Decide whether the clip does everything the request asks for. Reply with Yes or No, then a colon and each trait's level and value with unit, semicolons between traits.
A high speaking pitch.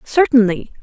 Yes: high, 240 Hz